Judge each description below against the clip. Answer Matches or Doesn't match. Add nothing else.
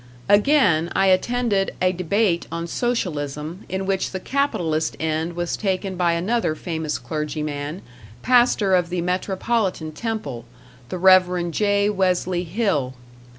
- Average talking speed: Doesn't match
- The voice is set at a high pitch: Doesn't match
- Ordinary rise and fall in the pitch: Matches